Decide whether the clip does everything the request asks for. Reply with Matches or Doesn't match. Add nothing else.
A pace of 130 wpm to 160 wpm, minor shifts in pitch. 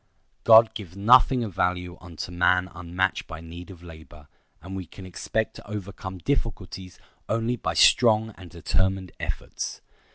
Doesn't match